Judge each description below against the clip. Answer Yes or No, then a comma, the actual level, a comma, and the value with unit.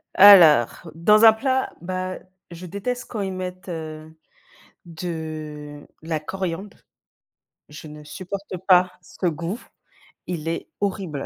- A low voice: No, medium, 175 Hz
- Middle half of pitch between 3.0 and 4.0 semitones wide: Yes, average, 3.5 semitones